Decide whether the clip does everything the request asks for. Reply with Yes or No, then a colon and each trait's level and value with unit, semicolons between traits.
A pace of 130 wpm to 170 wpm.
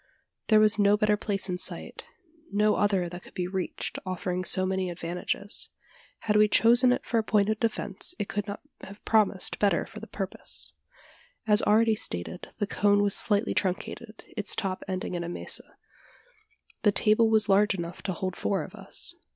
No: average, 185 wpm